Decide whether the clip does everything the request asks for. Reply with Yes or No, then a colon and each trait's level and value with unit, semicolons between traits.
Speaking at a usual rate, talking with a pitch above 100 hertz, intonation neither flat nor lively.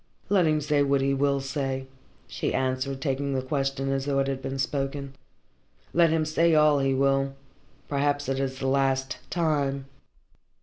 No: average, 170 wpm; low, 135 Hz; narrow, 1.2 semitones